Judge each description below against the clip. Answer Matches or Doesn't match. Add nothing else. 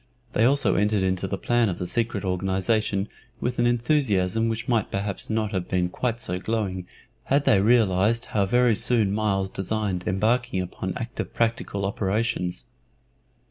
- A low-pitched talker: Matches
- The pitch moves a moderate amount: Matches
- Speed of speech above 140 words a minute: Matches